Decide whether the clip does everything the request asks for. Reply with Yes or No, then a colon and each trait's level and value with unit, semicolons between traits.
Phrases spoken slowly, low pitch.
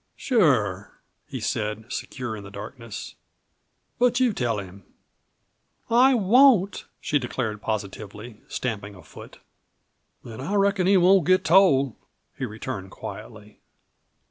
Yes: slow, 120 wpm; low, 125 Hz